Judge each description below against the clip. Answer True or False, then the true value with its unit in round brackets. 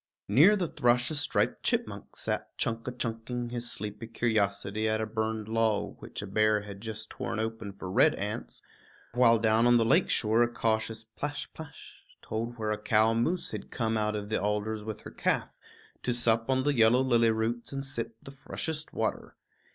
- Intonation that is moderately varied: False (1.9 semitones)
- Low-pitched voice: True (115 Hz)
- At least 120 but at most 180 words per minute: False (190 wpm)